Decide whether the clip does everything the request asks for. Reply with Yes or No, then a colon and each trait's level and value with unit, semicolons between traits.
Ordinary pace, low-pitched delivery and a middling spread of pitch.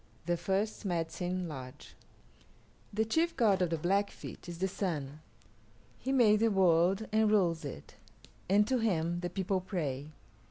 No: average, 150 wpm; medium, 185 Hz; average, 3.9 semitones